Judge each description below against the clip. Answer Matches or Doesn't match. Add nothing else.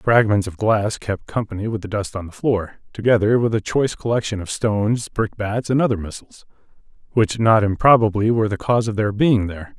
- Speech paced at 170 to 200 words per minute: Matches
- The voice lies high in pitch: Doesn't match